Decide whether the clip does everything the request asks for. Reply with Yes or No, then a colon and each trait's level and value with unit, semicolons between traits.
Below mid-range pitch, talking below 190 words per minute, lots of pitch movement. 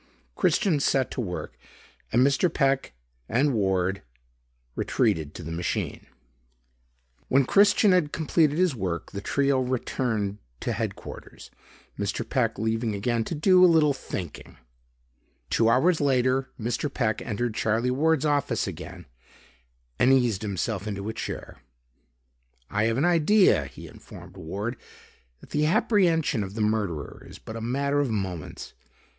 Yes: low, 125 Hz; average, 140 wpm; wide, 5.7 semitones